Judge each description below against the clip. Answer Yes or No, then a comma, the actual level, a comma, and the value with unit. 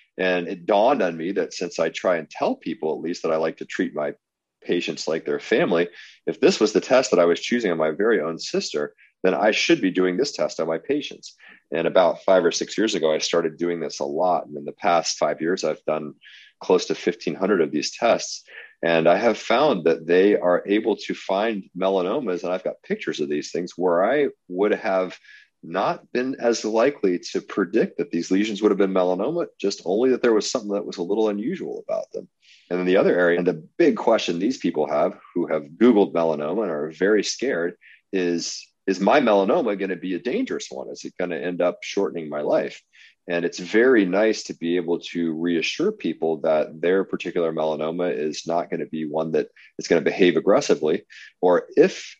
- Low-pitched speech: Yes, very low, 90 Hz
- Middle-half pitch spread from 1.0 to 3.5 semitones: Yes, narrow, 2.5 semitones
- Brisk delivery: Yes, fast, 220 wpm